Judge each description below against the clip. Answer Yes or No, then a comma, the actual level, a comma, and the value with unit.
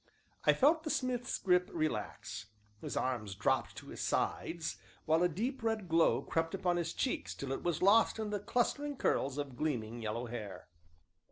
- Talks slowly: No, average, 175 wpm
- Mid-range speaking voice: Yes, medium, 170 Hz